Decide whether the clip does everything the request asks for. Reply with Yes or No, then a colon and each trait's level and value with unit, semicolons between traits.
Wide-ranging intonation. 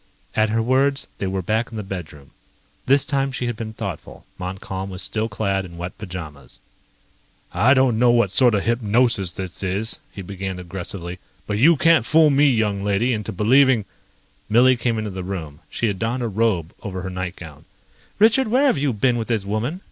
No: average, 4.7 semitones